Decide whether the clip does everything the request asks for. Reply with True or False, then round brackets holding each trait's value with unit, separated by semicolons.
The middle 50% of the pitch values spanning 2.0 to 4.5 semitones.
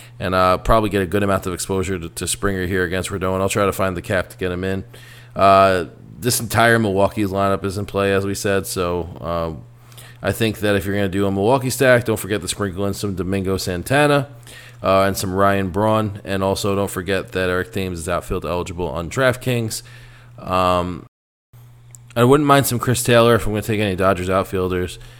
True (3.8 semitones)